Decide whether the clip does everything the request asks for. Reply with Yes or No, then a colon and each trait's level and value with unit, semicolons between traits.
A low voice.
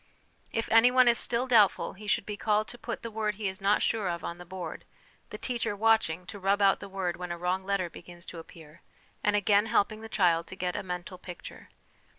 No: high, 200 Hz